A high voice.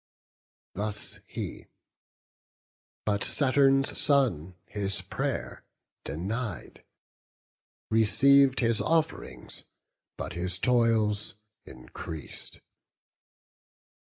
No: low, 110 Hz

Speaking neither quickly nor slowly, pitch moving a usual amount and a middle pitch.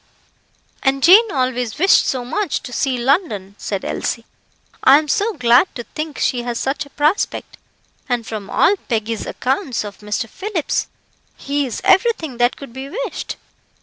No: average, 160 wpm; average, 4.7 semitones; very high, 265 Hz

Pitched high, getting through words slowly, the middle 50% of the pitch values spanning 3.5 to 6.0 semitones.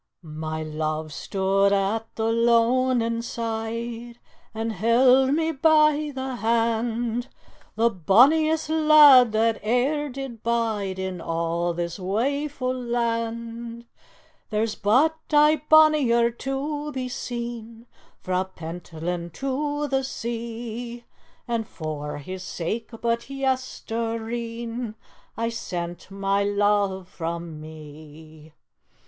Yes: high, 230 Hz; slow, 100 wpm; average, 4.9 semitones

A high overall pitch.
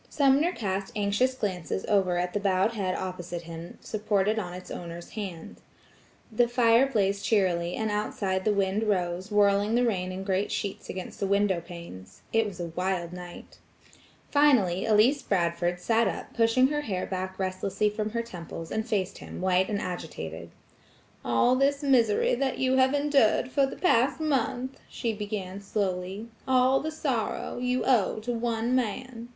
Yes: high, 205 Hz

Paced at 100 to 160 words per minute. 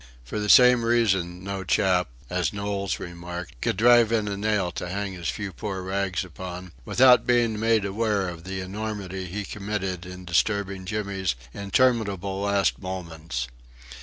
Yes: average, 155 wpm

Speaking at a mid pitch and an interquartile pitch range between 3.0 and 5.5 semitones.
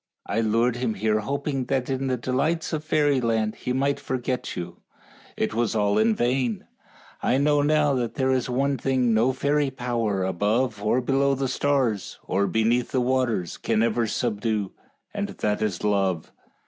No: low, 125 Hz; average, 3.9 semitones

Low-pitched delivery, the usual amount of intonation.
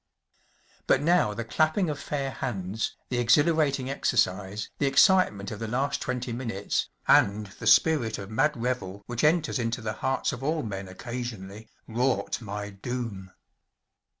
Yes: low, 120 Hz; average, 5.0 semitones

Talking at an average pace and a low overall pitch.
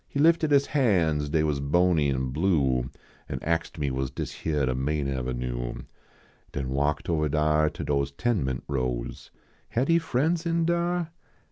Yes: average, 170 wpm; very low, 75 Hz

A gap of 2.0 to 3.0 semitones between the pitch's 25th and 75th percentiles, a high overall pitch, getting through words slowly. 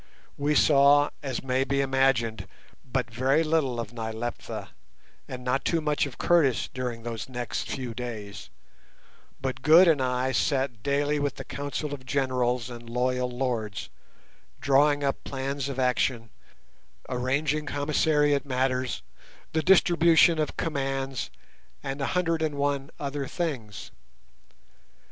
No: narrow, 2.6 semitones; low, 135 Hz; slow, 130 wpm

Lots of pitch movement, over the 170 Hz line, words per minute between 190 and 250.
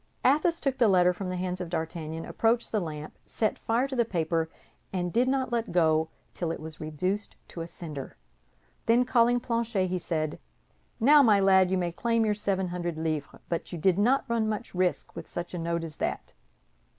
Yes: wide, 5.7 semitones; medium, 185 Hz; average, 200 wpm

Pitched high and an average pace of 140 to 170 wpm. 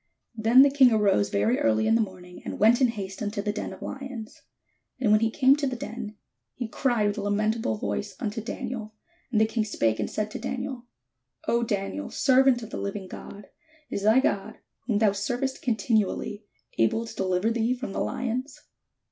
No: high, 220 Hz; average, 195 wpm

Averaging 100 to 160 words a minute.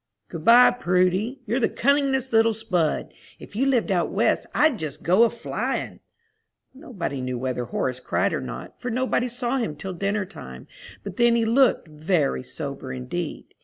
No: average, 170 wpm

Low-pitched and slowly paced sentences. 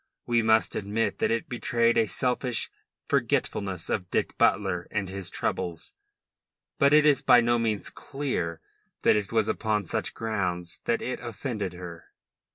No: low, 110 Hz; average, 155 wpm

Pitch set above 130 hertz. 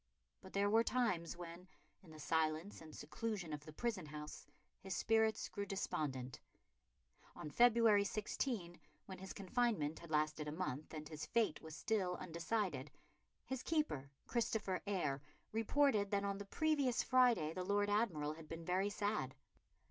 Yes: high, 190 Hz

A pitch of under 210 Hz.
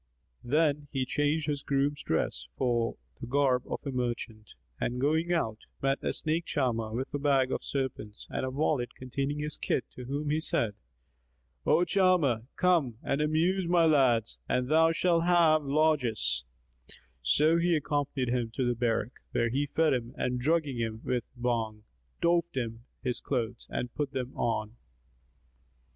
Yes: low, 135 Hz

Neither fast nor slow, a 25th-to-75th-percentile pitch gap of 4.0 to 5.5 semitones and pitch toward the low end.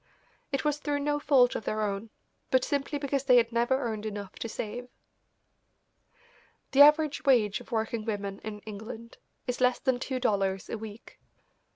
No: average, 170 wpm; average, 4.3 semitones; high, 240 Hz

